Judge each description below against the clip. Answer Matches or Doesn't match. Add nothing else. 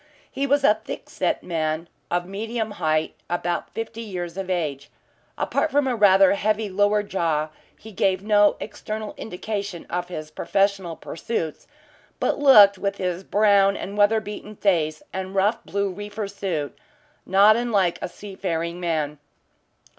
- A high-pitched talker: Matches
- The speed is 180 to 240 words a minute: Doesn't match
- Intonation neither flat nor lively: Matches